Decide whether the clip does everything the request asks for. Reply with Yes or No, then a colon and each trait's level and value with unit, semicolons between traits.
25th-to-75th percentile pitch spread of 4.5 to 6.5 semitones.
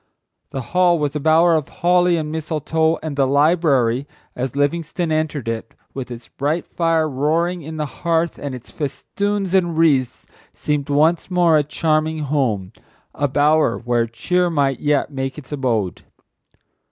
No: average, 3.5 semitones